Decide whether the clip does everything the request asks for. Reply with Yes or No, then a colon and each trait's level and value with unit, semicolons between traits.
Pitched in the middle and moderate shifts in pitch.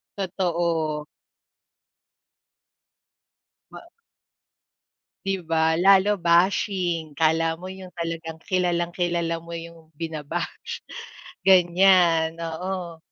No: medium, 170 Hz; narrow, 2.0 semitones